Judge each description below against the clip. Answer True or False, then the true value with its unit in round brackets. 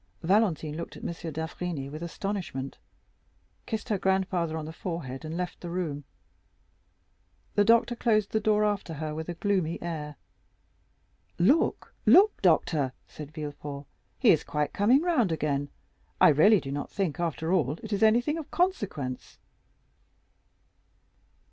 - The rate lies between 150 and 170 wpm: False (140 wpm)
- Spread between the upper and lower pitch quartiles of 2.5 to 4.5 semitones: False (5.2 semitones)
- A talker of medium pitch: True (170 Hz)